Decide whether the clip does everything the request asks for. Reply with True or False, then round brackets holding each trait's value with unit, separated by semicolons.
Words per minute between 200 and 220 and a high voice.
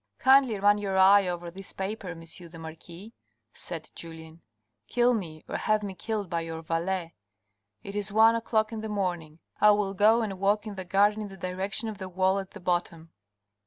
True (205 wpm; 195 Hz)